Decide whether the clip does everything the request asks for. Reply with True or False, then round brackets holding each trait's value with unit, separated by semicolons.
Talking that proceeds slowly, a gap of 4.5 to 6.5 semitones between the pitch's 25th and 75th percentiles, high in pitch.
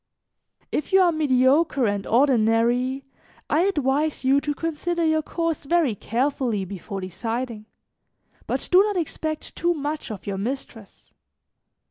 True (130 wpm; 5.6 semitones; 275 Hz)